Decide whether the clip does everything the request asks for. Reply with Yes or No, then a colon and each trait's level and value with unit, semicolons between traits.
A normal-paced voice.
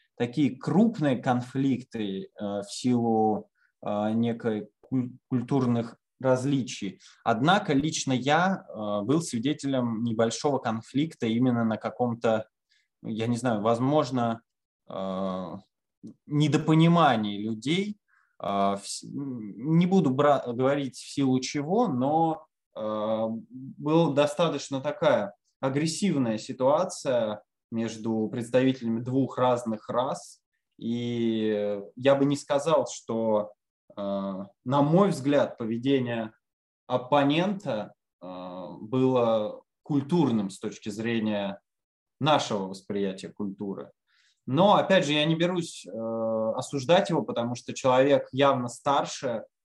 No: slow, 90 wpm